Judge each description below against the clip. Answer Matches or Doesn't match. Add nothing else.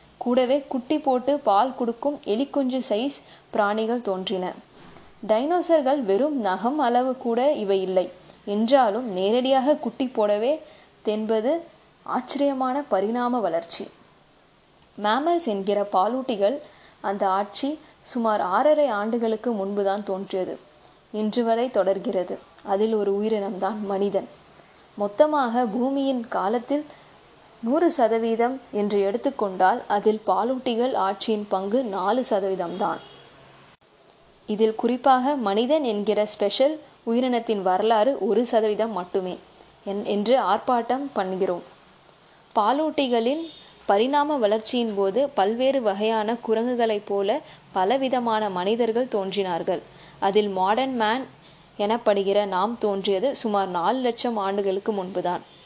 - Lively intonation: Doesn't match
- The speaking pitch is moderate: Doesn't match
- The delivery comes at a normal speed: Doesn't match